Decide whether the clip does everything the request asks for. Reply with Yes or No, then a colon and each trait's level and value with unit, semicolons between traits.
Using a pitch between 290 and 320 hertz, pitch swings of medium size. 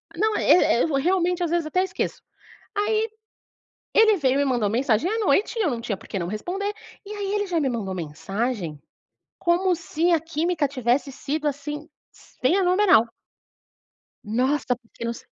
No: very high, 300 Hz; wide, 7.3 semitones